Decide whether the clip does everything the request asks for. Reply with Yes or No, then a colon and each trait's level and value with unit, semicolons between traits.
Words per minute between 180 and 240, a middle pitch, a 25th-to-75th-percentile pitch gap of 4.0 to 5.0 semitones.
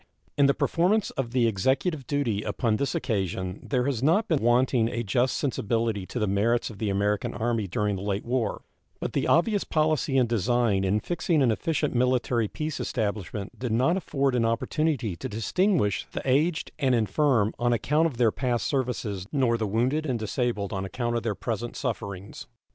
No: average, 185 wpm; low, 120 Hz; average, 4.5 semitones